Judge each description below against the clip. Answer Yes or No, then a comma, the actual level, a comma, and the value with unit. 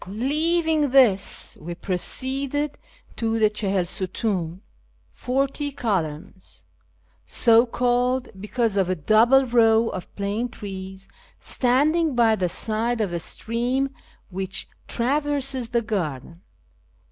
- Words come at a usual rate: No, slow, 115 wpm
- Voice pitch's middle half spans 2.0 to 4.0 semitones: No, average, 5.3 semitones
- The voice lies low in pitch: No, high, 230 Hz